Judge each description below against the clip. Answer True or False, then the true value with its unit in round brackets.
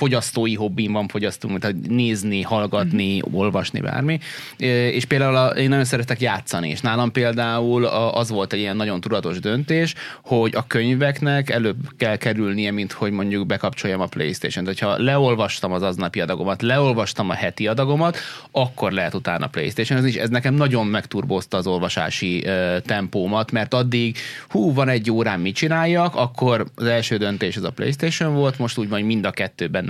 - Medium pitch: False (115 Hz)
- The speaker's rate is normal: False (165 wpm)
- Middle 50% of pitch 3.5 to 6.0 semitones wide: True (4.1 semitones)